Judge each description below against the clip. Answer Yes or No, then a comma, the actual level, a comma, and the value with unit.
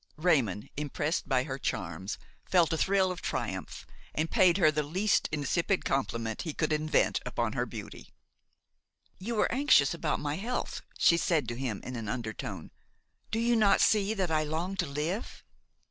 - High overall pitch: No, medium, 155 Hz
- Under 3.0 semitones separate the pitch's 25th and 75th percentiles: No, wide, 5.5 semitones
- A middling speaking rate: Yes, average, 170 wpm